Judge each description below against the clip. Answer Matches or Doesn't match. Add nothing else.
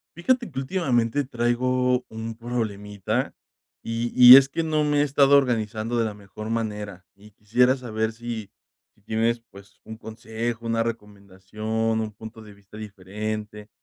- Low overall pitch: Matches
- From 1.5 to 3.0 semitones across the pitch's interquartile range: Matches